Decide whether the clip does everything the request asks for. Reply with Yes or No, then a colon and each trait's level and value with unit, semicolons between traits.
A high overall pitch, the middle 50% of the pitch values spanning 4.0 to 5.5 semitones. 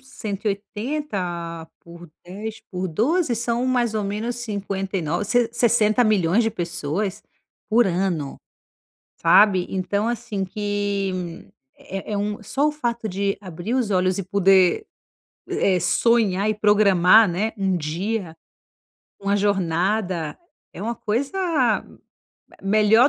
No: high, 200 Hz; average, 3.4 semitones